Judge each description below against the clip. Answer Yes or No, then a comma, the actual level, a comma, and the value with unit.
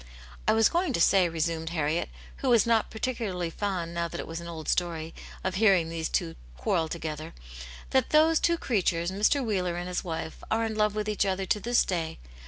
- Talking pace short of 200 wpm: No, fast, 205 wpm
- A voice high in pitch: No, medium, 180 Hz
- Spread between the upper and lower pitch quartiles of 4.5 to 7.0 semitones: Yes, average, 4.8 semitones